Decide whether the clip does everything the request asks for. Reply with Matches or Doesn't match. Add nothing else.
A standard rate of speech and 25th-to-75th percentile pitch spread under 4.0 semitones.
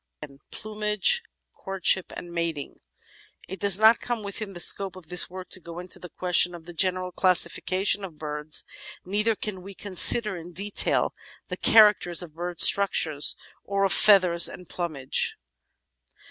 Matches